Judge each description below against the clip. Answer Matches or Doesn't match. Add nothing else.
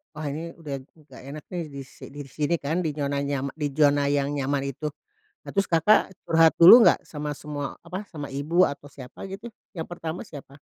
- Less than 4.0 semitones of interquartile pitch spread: Matches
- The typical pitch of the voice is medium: Matches